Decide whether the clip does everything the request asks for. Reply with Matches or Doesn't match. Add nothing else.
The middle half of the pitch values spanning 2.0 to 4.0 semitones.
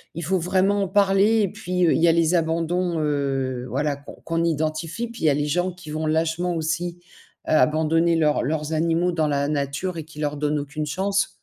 Matches